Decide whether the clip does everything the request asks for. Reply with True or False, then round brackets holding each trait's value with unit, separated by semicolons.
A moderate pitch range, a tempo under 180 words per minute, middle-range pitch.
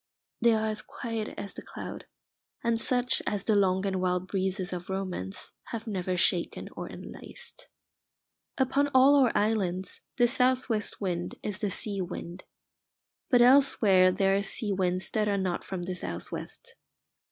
False (3.9 semitones; 165 wpm; 200 Hz)